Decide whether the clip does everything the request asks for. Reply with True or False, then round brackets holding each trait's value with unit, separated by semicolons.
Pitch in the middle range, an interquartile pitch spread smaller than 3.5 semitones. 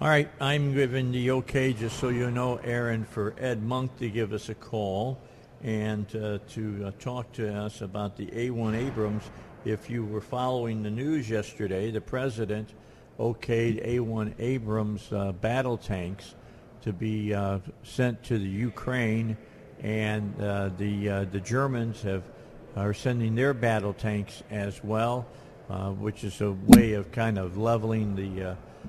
False (110 Hz; 2.9 semitones)